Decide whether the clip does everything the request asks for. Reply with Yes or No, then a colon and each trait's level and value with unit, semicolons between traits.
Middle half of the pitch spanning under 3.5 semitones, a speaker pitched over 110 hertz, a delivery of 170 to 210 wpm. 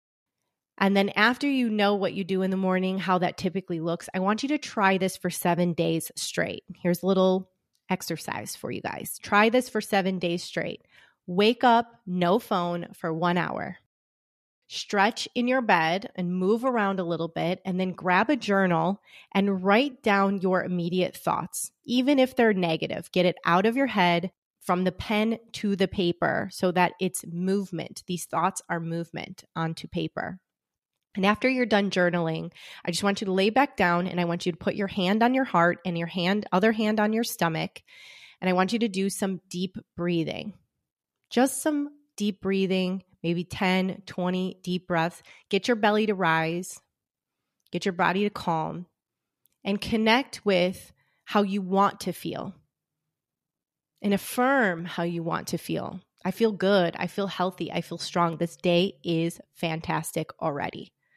Yes: average, 3.1 semitones; high, 190 Hz; average, 180 wpm